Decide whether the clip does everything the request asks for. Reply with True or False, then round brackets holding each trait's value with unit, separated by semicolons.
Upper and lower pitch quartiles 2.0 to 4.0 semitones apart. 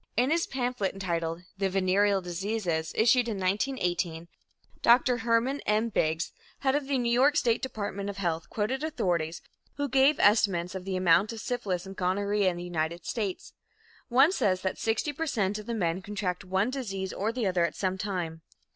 False (4.9 semitones)